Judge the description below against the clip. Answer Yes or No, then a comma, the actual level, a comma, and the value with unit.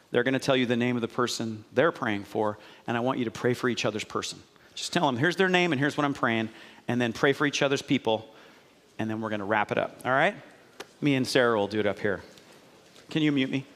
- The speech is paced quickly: Yes, fast, 275 wpm